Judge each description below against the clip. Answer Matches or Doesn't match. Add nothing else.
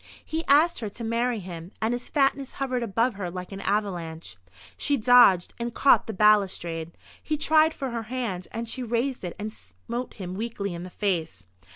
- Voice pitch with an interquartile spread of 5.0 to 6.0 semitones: Matches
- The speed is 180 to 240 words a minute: Matches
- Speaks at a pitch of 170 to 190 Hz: Doesn't match